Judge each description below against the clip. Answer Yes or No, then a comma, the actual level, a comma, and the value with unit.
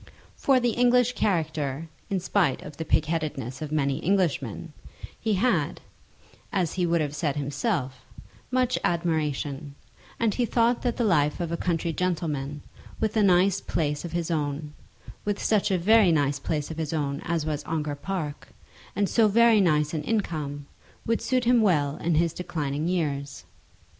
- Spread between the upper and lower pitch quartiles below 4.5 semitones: No, average, 5.2 semitones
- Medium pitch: Yes, medium, 165 Hz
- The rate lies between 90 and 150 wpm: No, average, 165 wpm